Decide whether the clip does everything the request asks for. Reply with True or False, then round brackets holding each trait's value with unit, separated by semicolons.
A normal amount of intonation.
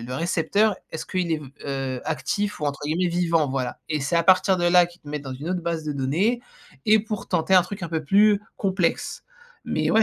True (4.2 semitones)